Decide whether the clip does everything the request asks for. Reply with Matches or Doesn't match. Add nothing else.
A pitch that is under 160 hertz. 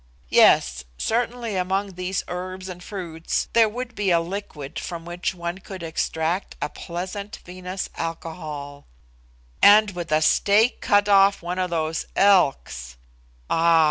Doesn't match